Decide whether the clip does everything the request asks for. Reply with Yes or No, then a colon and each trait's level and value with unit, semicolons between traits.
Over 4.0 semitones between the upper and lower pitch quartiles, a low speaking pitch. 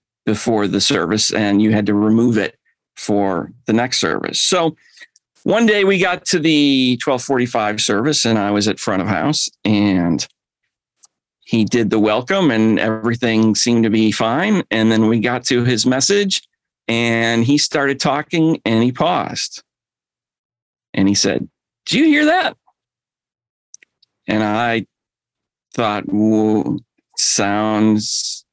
Yes: average, 4.7 semitones; low, 115 Hz